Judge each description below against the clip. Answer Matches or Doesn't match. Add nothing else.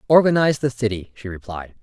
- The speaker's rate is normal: Matches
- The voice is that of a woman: Doesn't match